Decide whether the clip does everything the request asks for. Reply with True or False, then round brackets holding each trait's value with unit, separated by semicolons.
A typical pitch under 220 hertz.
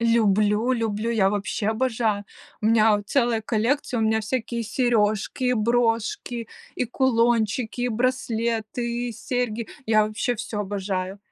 False (225 Hz)